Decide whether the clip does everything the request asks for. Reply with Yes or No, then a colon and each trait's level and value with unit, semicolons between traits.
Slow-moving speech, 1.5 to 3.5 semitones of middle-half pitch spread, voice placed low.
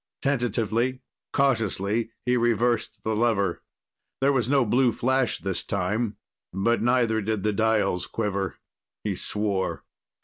Yes: slow, 125 wpm; average, 3.1 semitones; low, 110 Hz